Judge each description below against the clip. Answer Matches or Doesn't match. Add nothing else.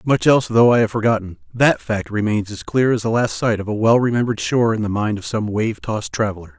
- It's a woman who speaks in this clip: Doesn't match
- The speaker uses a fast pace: Matches